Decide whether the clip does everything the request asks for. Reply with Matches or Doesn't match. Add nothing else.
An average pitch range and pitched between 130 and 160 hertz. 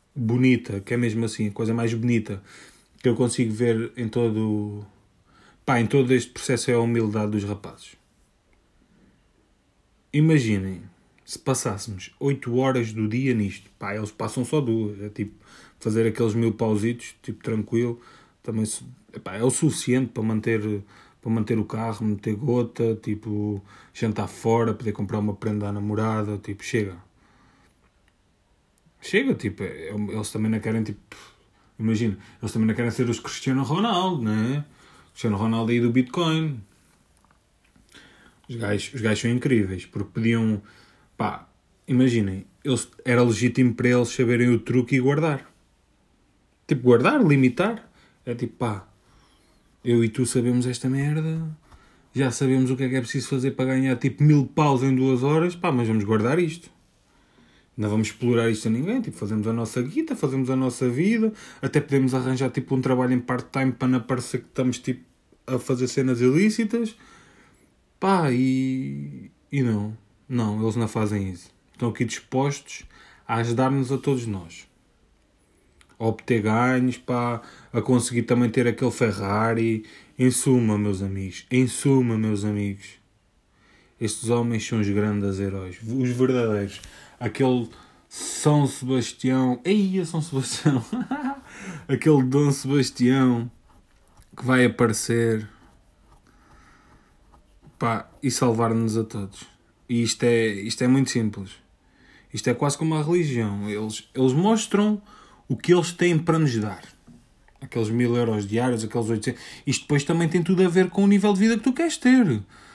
Doesn't match